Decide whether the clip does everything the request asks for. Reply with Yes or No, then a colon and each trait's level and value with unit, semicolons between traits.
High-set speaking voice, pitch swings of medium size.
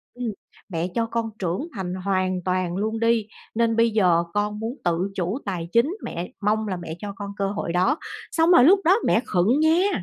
Yes: high, 210 Hz; average, 4.2 semitones